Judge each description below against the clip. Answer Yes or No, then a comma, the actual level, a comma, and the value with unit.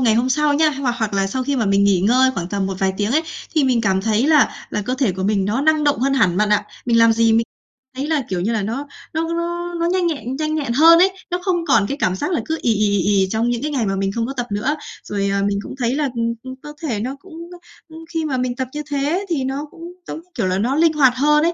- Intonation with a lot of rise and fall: Yes, wide, 6.4 semitones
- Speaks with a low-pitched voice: No, very high, 255 Hz